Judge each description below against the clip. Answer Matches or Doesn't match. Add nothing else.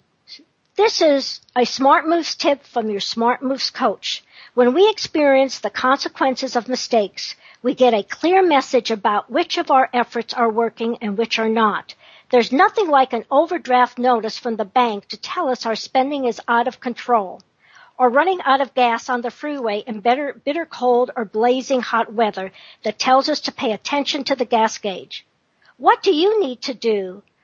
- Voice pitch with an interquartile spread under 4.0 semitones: Matches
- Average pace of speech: Matches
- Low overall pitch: Doesn't match